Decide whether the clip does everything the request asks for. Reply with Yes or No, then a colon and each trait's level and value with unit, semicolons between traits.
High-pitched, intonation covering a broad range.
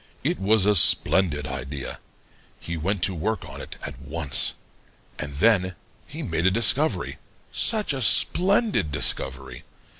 No: very low, 95 Hz; wide, 7.2 semitones